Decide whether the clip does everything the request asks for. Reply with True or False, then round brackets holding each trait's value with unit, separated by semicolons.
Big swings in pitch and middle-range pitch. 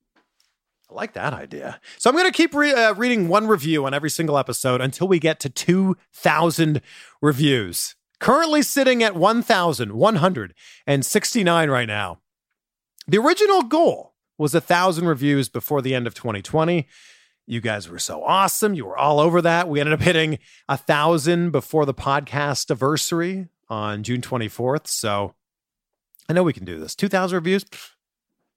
True (6.0 semitones; 155 Hz)